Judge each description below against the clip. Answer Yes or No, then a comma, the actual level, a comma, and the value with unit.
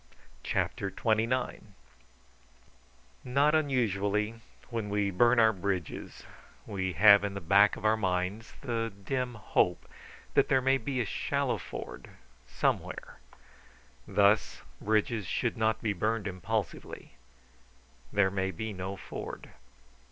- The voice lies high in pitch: No, low, 105 Hz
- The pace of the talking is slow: Yes, slow, 120 wpm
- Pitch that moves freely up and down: No, average, 2.7 semitones